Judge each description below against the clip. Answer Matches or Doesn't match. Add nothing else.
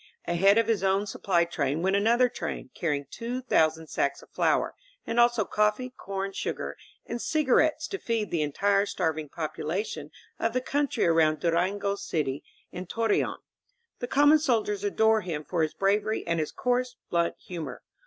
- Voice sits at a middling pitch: Doesn't match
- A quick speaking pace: Doesn't match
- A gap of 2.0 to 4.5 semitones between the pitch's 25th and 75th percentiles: Doesn't match